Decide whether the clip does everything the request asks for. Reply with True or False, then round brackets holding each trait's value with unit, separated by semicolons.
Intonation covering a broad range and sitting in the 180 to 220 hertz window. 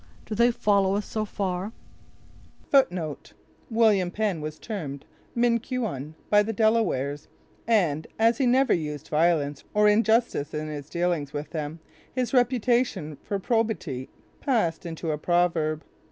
True (6.5 semitones; 185 Hz)